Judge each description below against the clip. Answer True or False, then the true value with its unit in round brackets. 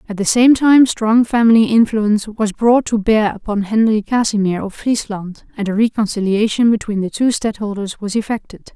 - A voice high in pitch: True (215 Hz)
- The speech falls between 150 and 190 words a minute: True (170 wpm)